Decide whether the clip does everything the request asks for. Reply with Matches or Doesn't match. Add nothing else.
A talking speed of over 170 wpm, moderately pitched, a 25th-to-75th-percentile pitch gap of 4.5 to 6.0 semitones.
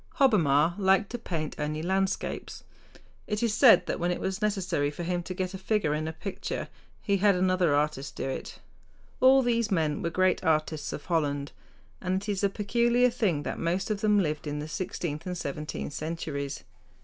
Matches